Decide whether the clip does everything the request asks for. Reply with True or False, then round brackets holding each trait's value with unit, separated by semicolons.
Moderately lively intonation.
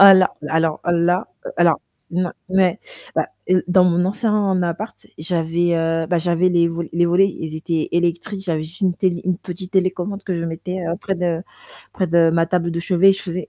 False (1.7 semitones)